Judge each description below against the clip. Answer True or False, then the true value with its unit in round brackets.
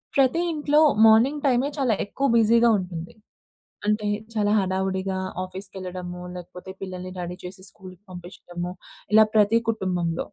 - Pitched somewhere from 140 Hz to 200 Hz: True (190 Hz)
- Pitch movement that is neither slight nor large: True (3.7 semitones)